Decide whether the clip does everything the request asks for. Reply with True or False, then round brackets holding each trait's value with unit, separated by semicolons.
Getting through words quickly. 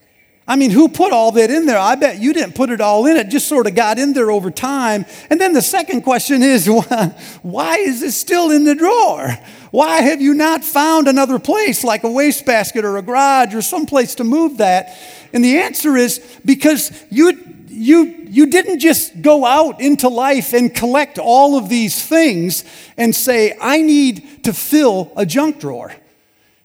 False (195 wpm)